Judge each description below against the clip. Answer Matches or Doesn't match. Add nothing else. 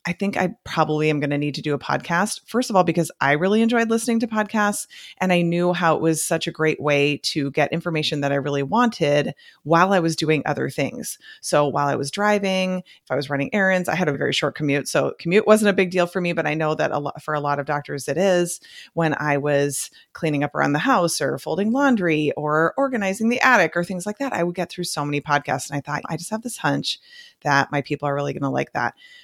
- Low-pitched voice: Doesn't match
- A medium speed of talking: Doesn't match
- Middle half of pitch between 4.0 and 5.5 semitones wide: Matches